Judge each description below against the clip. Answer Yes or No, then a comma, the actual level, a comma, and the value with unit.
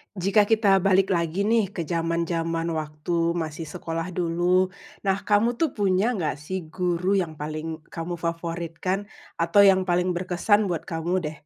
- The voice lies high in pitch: No, medium, 175 Hz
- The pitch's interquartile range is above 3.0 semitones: No, narrow, 2.6 semitones